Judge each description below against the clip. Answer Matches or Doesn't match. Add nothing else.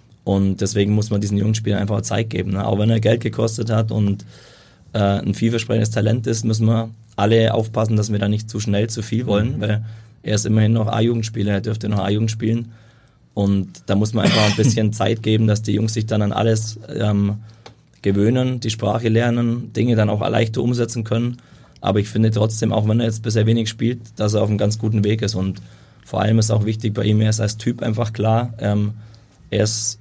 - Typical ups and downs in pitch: Doesn't match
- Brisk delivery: Matches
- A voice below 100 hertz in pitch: Doesn't match